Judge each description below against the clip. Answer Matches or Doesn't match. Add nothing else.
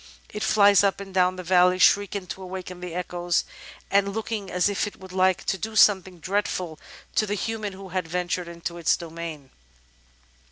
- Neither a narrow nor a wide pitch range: Doesn't match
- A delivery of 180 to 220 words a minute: Matches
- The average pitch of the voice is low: Doesn't match